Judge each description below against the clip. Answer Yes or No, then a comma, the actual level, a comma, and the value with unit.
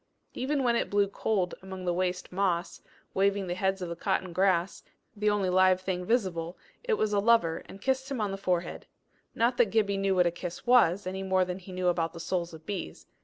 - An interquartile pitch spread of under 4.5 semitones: Yes, narrow, 2.4 semitones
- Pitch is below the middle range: No, high, 190 Hz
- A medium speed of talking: No, fast, 220 wpm